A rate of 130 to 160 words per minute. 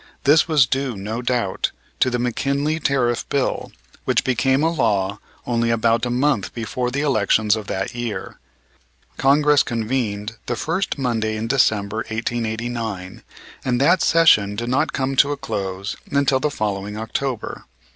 Yes: average, 150 wpm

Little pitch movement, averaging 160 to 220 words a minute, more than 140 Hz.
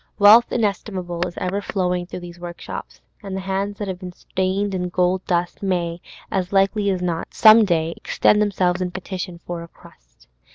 Yes: narrow, 2.0 semitones; average, 180 wpm; medium, 185 Hz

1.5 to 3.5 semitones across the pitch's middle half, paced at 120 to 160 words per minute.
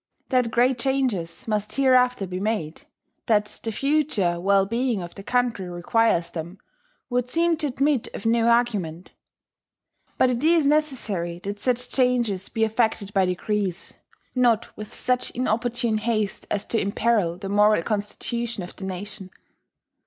No: average, 4.2 semitones; average, 145 wpm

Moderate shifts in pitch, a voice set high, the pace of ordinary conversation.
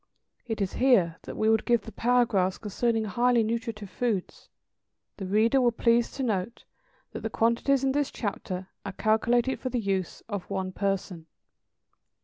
Yes: average, 3.5 semitones; high, 220 Hz; average, 160 wpm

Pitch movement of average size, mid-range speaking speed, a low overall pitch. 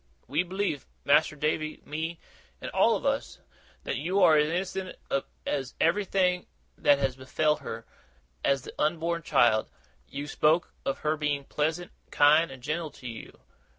No: average, 3.2 semitones; average, 150 wpm; medium, 155 Hz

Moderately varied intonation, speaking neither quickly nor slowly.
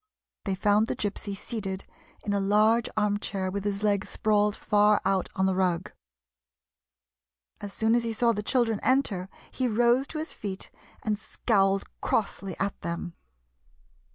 No: narrow, 2.3 semitones; average, 155 wpm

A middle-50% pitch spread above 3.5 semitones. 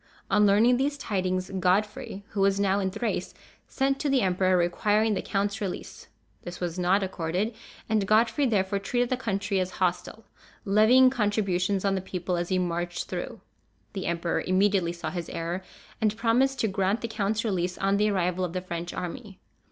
No: average, 2.9 semitones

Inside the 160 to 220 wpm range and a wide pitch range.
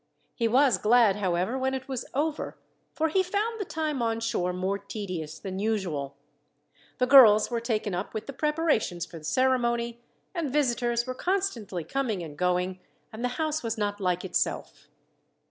Yes: average, 170 wpm; wide, 5.9 semitones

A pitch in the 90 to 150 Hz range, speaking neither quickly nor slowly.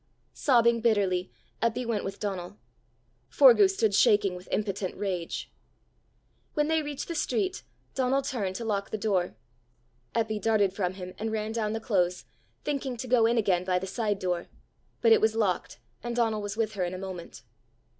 No: high, 215 Hz; average, 175 wpm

